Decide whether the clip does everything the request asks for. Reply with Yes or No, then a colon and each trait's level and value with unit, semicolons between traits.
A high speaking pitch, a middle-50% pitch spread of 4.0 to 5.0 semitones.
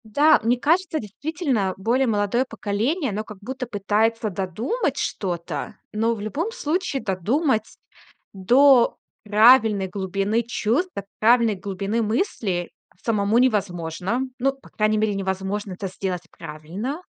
Yes: high, 215 Hz; average, 4.6 semitones